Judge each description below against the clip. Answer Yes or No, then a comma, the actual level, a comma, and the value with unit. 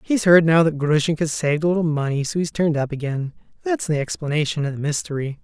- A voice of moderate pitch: Yes, medium, 155 Hz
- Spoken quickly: Yes, fast, 210 wpm